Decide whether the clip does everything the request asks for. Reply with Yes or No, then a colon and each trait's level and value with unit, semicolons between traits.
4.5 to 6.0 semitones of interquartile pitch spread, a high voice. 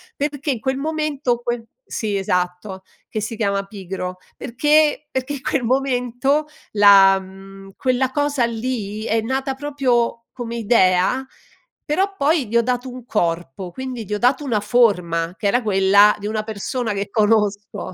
Yes: average, 4.8 semitones; high, 230 Hz